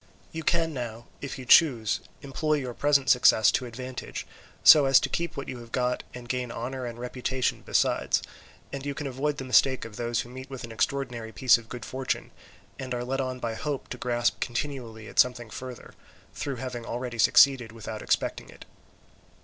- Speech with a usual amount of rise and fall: No, narrow, 2.2 semitones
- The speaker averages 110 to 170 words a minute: No, average, 190 wpm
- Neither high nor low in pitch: No, low, 125 Hz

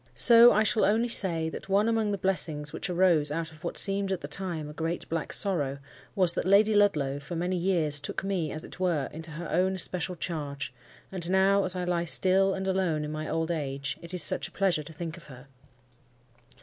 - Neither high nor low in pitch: Yes, medium, 175 Hz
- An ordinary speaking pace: No, fast, 220 wpm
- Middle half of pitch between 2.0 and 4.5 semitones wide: Yes, average, 3.7 semitones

